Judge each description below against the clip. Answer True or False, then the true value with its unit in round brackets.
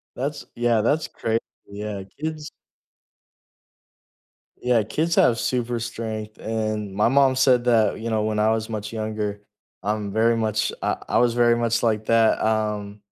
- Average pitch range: False (1.9 semitones)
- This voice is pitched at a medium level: False (110 Hz)